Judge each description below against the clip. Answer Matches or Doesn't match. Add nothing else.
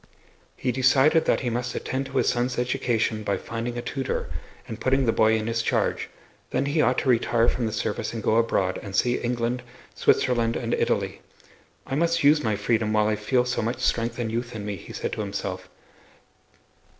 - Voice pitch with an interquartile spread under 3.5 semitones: Matches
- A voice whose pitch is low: Matches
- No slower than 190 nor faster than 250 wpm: Matches